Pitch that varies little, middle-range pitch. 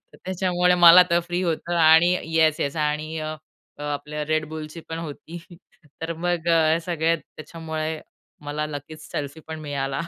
Yes: narrow, 1.9 semitones; medium, 160 Hz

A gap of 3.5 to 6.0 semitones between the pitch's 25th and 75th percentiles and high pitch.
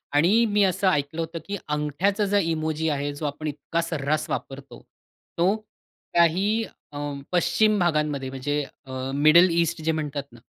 No: average, 3.9 semitones; medium, 160 Hz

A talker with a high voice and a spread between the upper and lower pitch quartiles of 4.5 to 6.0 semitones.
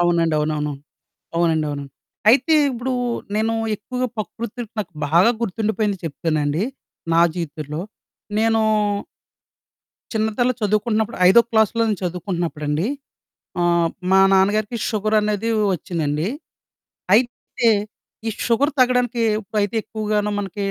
Yes: high, 205 Hz; average, 5.0 semitones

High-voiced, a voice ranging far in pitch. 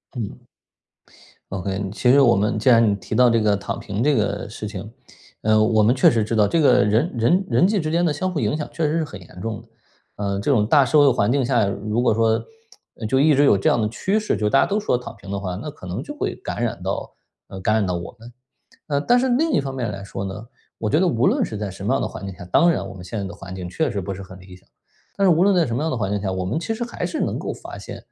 No: low, 110 Hz; wide, 6.4 semitones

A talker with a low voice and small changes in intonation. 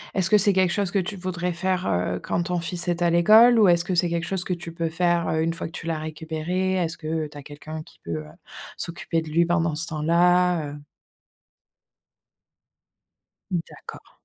No: medium, 170 Hz; narrow, 2.1 semitones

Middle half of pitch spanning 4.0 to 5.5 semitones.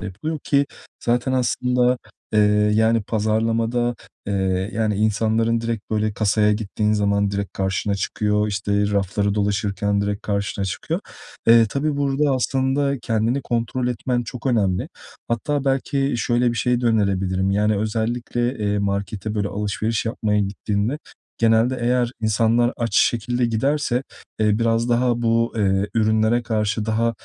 No: average, 2.8 semitones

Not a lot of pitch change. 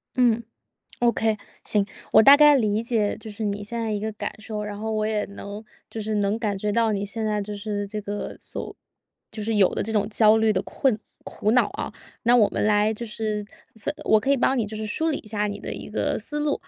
Yes: narrow, 1.6 semitones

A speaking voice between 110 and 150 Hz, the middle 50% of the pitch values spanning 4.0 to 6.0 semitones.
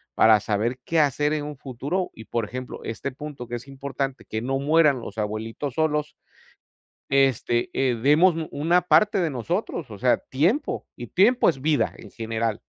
Yes: low, 135 Hz; average, 4.5 semitones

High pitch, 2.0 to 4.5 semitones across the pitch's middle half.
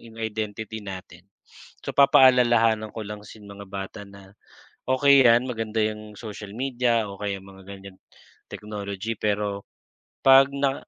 No: low, 110 Hz; average, 2.9 semitones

